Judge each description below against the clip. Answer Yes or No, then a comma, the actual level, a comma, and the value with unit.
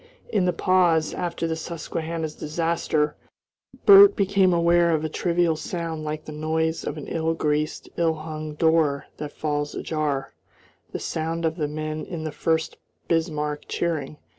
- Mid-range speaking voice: Yes, medium, 160 Hz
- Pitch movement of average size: No, narrow, 1.7 semitones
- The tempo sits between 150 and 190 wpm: Yes, average, 155 wpm